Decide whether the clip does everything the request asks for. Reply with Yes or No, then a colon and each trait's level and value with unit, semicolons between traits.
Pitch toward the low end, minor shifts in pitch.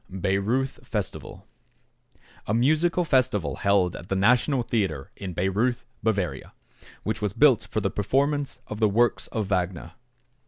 No: low, 105 Hz; average, 4.7 semitones